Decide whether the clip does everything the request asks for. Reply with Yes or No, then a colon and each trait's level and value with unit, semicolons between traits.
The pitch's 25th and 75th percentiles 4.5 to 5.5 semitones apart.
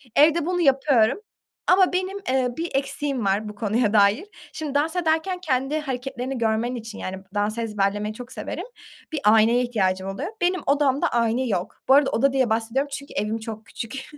Yes: average, 4.9 semitones